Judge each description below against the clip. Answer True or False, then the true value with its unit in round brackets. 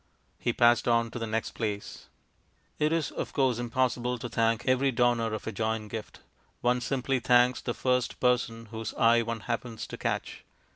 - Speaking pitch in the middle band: False (120 Hz)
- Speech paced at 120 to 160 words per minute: False (180 wpm)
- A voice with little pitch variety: True (1.7 semitones)